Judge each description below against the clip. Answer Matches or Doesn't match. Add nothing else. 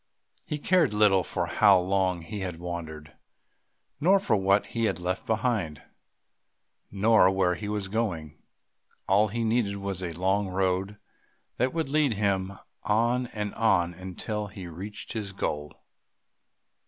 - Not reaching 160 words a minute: Matches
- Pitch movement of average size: Matches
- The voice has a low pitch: Matches